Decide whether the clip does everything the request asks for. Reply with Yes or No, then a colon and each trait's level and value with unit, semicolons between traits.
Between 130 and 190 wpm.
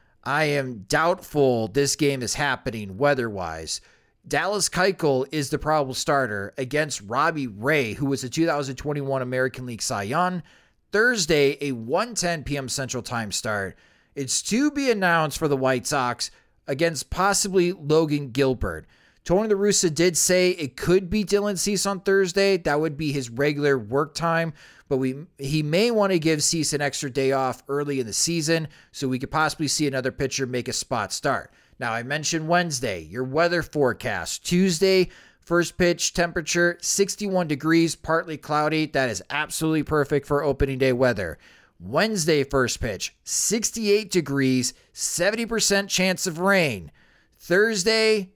Yes: average, 155 wpm